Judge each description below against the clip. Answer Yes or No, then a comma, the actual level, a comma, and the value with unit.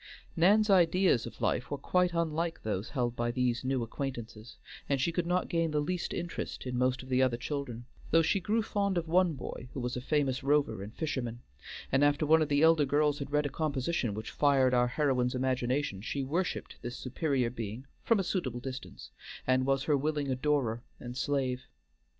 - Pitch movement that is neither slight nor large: Yes, average, 4.3 semitones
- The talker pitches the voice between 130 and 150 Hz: Yes, medium, 140 Hz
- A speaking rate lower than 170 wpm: No, average, 195 wpm